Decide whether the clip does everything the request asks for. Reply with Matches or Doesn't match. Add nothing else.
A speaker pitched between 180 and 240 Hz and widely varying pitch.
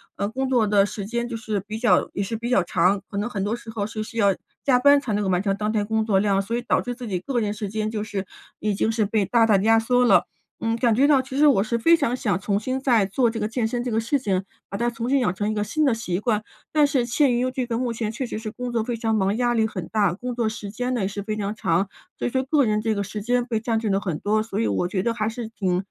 Doesn't match